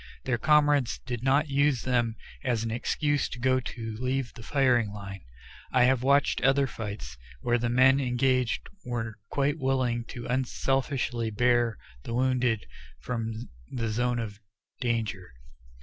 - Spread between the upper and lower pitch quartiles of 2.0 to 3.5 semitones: Yes, narrow, 2.6 semitones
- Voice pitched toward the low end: Yes, low, 125 Hz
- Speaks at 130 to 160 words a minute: Yes, average, 145 wpm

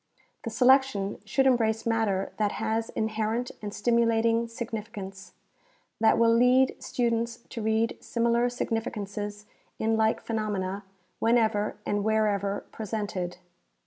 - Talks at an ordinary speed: No, slow, 115 wpm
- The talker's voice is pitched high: Yes, high, 220 Hz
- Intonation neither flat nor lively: No, narrow, 2.0 semitones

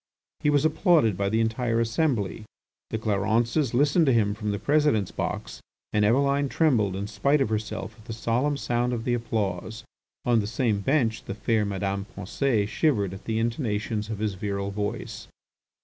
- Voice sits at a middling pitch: No, low, 110 Hz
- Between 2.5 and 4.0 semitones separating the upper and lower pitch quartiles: Yes, average, 3.7 semitones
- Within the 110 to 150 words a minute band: No, average, 175 wpm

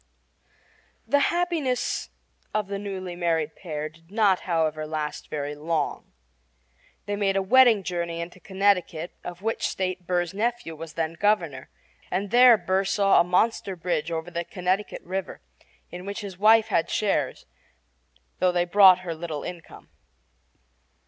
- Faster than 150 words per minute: No, average, 145 wpm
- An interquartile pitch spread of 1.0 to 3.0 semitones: No, average, 3.5 semitones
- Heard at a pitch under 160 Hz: No, medium, 180 Hz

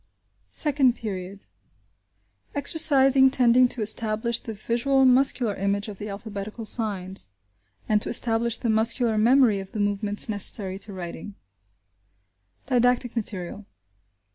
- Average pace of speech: No, slow, 115 wpm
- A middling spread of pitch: Yes, average, 3.4 semitones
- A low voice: No, high, 220 Hz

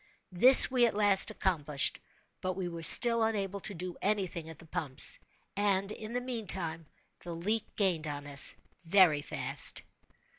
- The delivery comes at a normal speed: Yes, average, 155 wpm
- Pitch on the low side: No, medium, 185 Hz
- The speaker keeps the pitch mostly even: No, average, 4.3 semitones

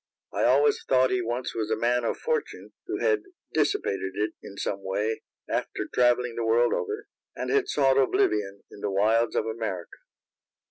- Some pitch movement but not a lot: Yes, average, 3.9 semitones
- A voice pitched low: Yes, low, 115 Hz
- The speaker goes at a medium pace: Yes, average, 175 wpm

